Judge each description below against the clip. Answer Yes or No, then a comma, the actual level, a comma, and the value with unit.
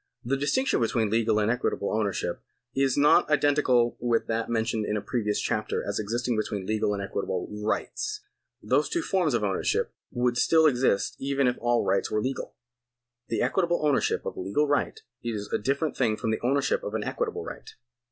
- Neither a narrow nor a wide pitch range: Yes, average, 4.4 semitones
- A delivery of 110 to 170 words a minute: No, average, 185 wpm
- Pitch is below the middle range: Yes, low, 120 Hz